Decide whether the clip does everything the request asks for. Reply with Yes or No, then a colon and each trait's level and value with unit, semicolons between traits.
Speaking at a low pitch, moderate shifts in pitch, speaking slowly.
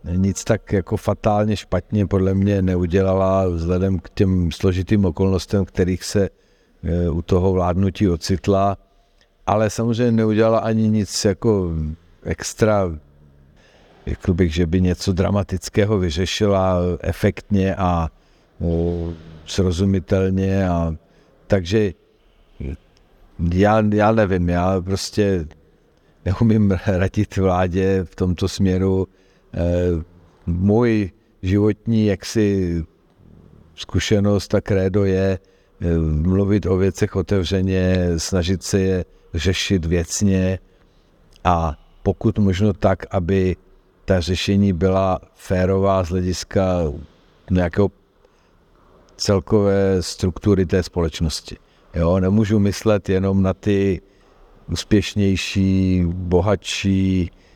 No: very low, 95 Hz; narrow, 2.0 semitones; slow, 90 wpm